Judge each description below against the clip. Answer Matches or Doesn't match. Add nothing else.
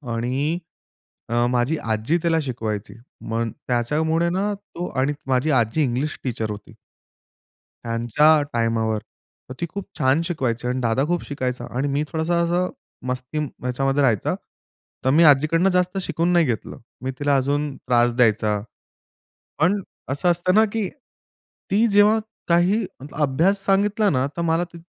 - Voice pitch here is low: Doesn't match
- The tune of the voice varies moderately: Doesn't match